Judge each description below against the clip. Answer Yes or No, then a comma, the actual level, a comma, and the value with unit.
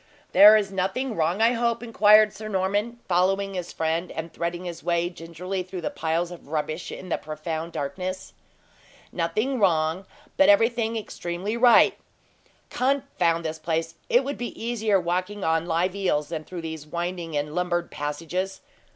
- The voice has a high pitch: No, medium, 180 Hz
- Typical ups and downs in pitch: Yes, average, 4.1 semitones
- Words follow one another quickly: No, average, 160 wpm